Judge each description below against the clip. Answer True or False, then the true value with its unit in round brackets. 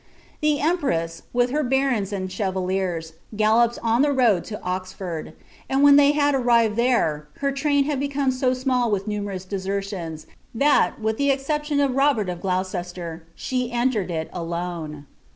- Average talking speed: True (160 wpm)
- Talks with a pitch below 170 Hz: False (220 Hz)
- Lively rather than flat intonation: True (6.7 semitones)